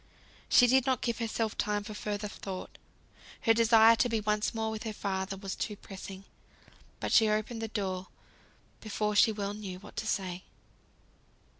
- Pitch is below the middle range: No, high, 210 Hz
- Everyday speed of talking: Yes, average, 170 wpm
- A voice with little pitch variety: Yes, narrow, 2.1 semitones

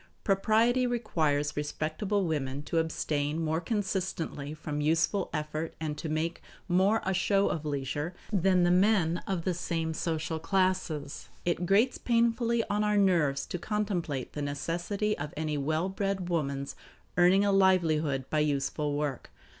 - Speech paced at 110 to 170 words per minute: Yes, average, 150 wpm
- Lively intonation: No, average, 4.4 semitones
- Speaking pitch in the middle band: Yes, medium, 165 Hz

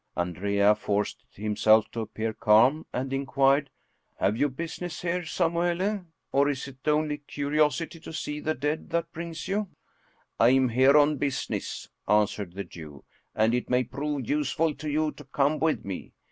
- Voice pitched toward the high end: No, medium, 140 Hz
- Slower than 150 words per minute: No, average, 175 wpm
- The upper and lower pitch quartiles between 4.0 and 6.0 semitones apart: Yes, wide, 5.6 semitones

